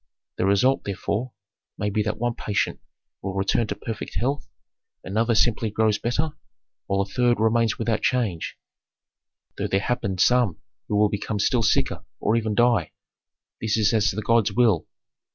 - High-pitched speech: No, low, 110 Hz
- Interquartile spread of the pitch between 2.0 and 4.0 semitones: Yes, average, 2.8 semitones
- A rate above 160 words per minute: No, average, 155 wpm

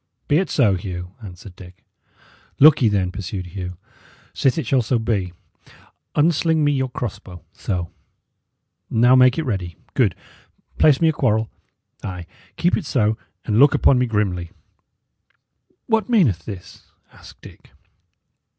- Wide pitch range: Yes, wide, 7.2 semitones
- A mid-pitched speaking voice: No, low, 110 Hz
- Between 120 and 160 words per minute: Yes, average, 145 wpm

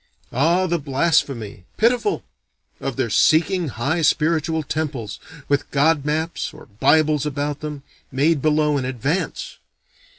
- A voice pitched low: No, medium, 150 Hz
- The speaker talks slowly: Yes, slow, 125 wpm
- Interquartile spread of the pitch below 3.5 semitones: Yes, average, 2.8 semitones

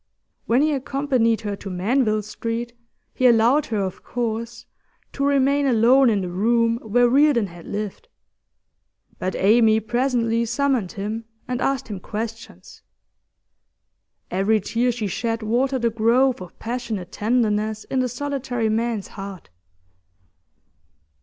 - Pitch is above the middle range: Yes, high, 230 Hz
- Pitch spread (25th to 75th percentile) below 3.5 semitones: Yes, average, 2.8 semitones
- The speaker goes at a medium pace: No, slow, 130 wpm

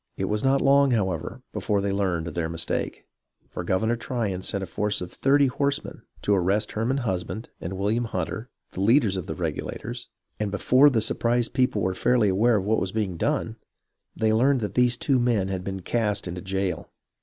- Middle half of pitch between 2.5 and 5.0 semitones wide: Yes, average, 4.3 semitones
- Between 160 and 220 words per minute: Yes, average, 195 wpm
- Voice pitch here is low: Yes, low, 105 Hz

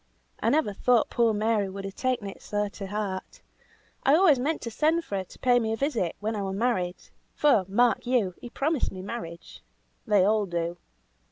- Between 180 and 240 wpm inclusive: Yes, average, 200 wpm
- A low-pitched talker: No, high, 215 Hz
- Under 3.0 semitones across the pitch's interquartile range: No, average, 4.3 semitones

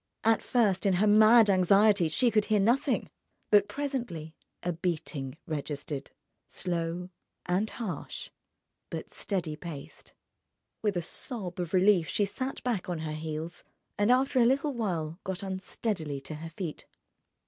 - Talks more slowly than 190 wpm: Yes, average, 145 wpm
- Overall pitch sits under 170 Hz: No, medium, 185 Hz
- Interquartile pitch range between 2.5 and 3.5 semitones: No, average, 4.8 semitones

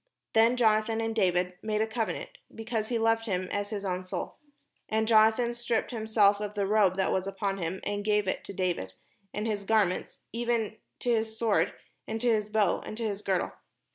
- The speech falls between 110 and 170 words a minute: No, average, 200 wpm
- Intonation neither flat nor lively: No, narrow, 2.3 semitones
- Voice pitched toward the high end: Yes, high, 215 Hz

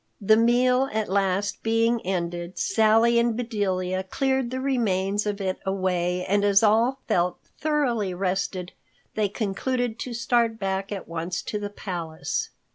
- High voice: Yes, high, 205 Hz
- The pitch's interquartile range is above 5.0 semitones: No, average, 3.9 semitones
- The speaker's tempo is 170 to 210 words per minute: No, average, 145 wpm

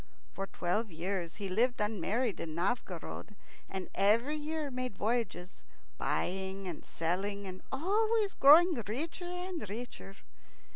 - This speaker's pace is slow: Yes, slow, 125 wpm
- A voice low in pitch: No, high, 215 Hz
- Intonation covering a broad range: Yes, wide, 7.0 semitones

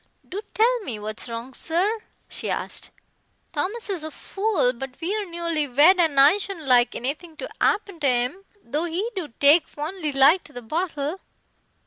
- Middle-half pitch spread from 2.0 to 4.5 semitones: No, wide, 5.6 semitones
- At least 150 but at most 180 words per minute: Yes, average, 170 wpm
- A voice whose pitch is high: Yes, very high, 315 Hz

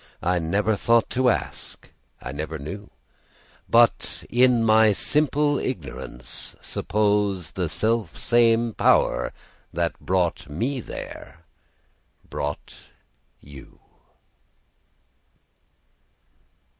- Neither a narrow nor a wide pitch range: No, wide, 6.1 semitones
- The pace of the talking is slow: Yes, slow, 80 wpm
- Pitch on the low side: Yes, low, 105 Hz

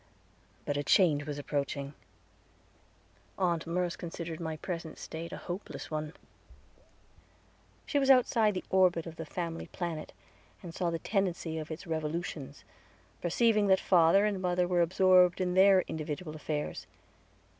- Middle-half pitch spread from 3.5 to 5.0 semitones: No, average, 2.8 semitones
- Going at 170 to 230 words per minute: No, average, 140 wpm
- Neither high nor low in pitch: Yes, medium, 170 Hz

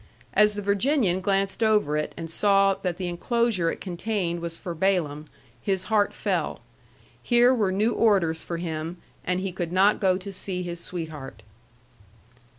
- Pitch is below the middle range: No, medium, 185 Hz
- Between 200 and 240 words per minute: No, average, 160 wpm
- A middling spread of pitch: Yes, average, 3.3 semitones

